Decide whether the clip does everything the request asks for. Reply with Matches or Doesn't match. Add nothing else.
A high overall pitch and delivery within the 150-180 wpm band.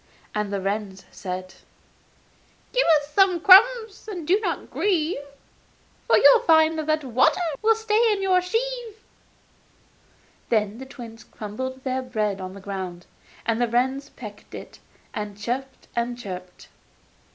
Doesn't match